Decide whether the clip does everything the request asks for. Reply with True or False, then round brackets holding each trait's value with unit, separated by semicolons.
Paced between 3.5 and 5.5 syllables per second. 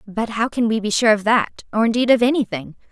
False (5.8 syllables/s)